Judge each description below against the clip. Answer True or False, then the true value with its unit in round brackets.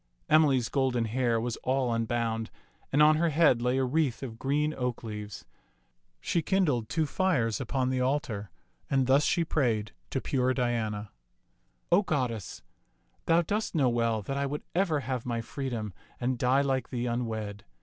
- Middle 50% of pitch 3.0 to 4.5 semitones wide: True (3.9 semitones)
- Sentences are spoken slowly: False (170 wpm)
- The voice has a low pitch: True (130 Hz)